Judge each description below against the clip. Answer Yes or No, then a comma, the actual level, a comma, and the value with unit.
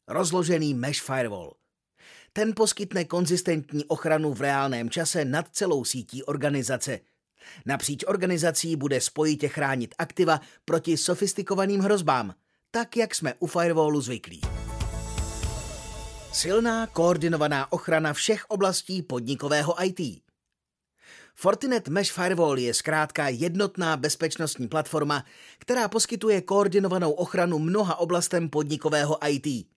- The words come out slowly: Yes, slow, 105 wpm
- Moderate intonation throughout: Yes, average, 4.5 semitones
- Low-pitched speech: No, medium, 160 Hz